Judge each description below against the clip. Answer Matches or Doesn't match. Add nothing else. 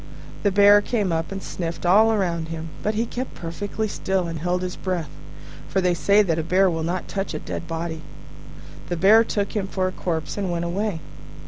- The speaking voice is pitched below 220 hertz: Matches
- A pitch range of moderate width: Matches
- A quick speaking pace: Matches